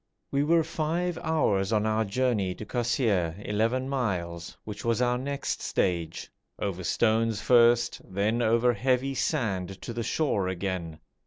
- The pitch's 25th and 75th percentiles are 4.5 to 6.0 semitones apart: Yes, average, 4.8 semitones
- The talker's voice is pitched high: No, low, 115 Hz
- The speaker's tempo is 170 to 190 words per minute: No, average, 145 wpm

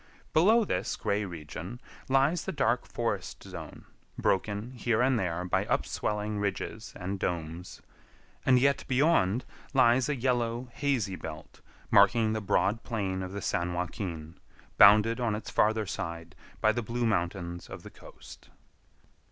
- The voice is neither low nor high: No, low, 105 Hz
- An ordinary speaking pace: Yes, average, 145 wpm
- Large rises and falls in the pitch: No, average, 5.0 semitones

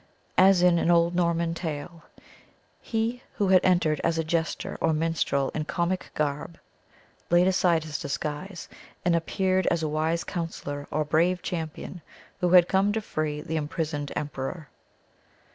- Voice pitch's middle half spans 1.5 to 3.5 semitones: Yes, average, 2.7 semitones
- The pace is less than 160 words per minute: Yes, average, 150 wpm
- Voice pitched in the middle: Yes, medium, 165 Hz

